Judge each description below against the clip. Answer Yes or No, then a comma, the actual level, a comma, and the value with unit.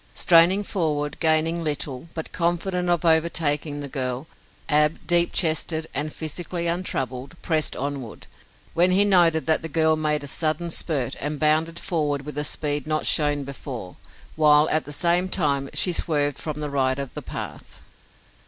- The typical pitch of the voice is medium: Yes, medium, 155 Hz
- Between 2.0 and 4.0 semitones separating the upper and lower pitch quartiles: Yes, narrow, 2.6 semitones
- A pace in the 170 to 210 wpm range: No, average, 160 wpm